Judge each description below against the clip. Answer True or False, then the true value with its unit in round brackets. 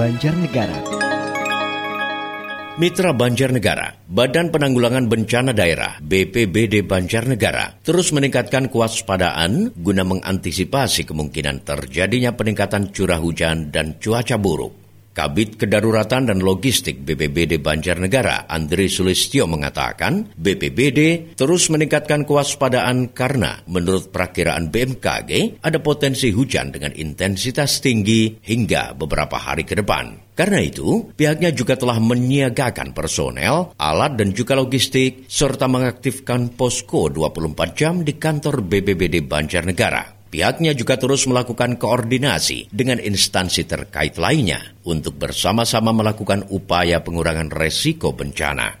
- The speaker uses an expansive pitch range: True (6.7 semitones)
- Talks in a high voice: False (110 Hz)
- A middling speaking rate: True (105 wpm)